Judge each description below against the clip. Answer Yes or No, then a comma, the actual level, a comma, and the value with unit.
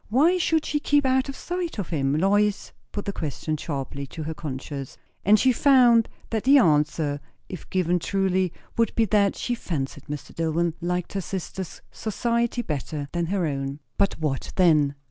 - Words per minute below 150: No, average, 175 wpm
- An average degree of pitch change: No, wide, 7.2 semitones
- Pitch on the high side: No, medium, 180 Hz